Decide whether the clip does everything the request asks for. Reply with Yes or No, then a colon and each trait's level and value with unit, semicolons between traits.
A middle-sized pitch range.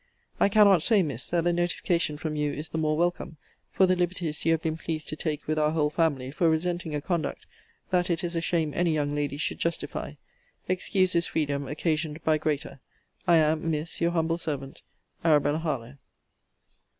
No: narrow, 2.3 semitones